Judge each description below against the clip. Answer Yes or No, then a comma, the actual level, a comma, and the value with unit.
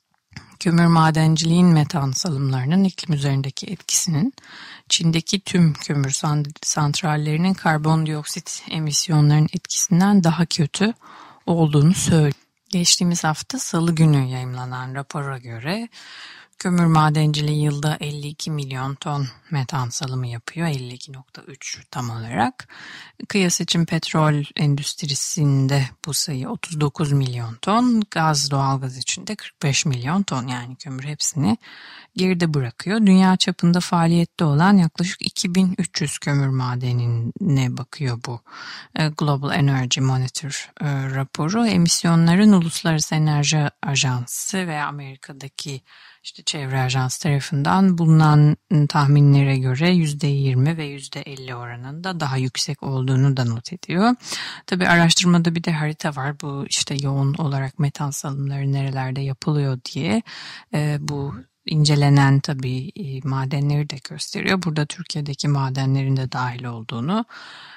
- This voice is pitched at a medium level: Yes, medium, 150 Hz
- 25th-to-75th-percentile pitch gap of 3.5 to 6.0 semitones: Yes, average, 4.0 semitones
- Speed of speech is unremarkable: Yes, average, 110 wpm